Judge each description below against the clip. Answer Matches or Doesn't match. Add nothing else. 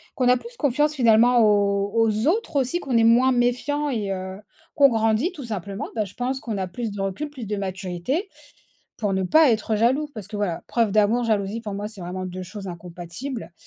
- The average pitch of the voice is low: Doesn't match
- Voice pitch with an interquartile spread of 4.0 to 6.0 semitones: Matches